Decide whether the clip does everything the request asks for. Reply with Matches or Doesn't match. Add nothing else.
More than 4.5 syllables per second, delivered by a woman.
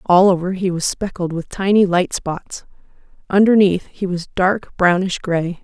Doesn't match